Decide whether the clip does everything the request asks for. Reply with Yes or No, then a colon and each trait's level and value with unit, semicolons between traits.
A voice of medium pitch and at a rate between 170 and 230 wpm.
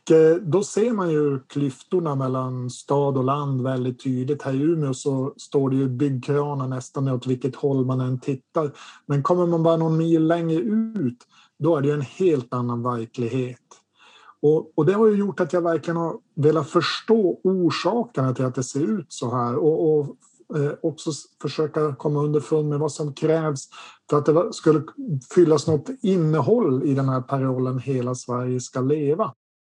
Yes: medium, 145 Hz; average, 180 wpm